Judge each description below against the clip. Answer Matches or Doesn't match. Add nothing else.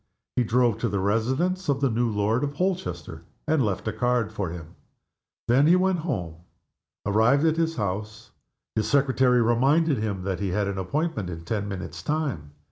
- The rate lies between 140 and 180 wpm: Matches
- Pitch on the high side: Doesn't match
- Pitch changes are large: Matches